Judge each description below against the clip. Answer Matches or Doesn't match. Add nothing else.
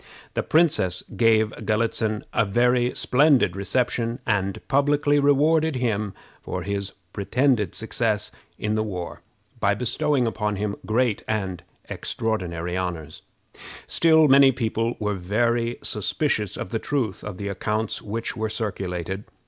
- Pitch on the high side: Doesn't match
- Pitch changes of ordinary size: Matches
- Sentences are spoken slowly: Matches